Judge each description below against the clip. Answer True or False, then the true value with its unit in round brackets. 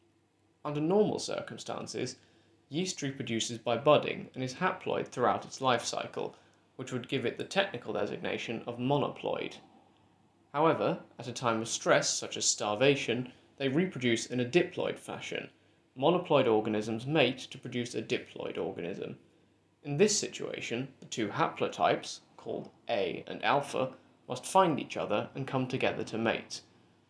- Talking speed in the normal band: True (145 wpm)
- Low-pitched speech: True (130 Hz)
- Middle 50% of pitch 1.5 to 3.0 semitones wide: False (4.4 semitones)